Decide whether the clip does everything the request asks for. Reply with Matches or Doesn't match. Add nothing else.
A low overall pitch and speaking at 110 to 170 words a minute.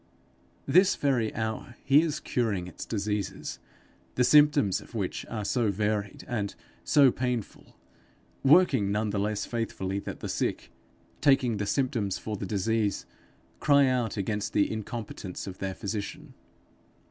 Matches